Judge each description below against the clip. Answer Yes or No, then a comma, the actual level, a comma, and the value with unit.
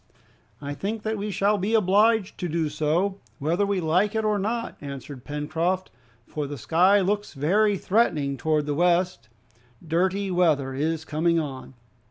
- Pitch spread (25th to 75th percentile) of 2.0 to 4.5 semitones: No, average, 5.2 semitones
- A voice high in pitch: No, medium, 175 Hz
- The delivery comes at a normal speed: Yes, average, 160 wpm